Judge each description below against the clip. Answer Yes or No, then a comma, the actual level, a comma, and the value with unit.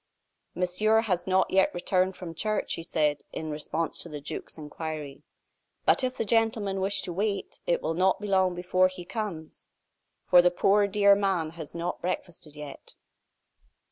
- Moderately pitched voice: Yes, medium, 180 Hz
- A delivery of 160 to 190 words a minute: Yes, average, 170 wpm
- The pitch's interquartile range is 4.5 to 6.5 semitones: No, average, 3.4 semitones